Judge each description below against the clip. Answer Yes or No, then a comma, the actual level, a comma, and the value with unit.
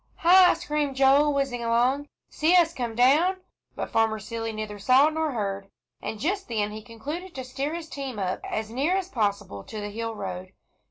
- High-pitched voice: Yes, very high, 255 Hz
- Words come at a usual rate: Yes, average, 185 wpm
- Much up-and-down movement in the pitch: Yes, wide, 5.8 semitones